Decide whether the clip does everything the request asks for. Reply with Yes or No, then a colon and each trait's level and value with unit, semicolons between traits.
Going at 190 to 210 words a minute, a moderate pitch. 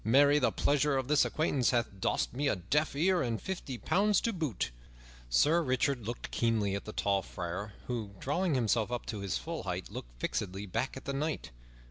No: average, 195 wpm; low, 125 Hz